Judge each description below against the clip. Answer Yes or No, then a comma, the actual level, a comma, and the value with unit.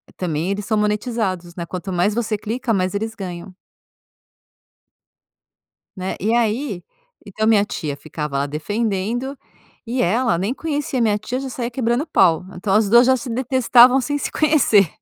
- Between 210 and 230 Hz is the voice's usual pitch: Yes, high, 215 Hz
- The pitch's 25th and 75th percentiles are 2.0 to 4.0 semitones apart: No, average, 4.8 semitones